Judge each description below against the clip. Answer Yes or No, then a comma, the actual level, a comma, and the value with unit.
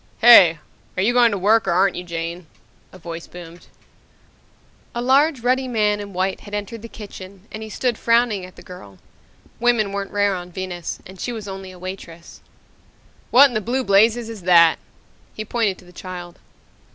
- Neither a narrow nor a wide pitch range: Yes, average, 4.1 semitones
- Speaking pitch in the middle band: No, high, 200 Hz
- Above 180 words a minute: Yes, average, 190 wpm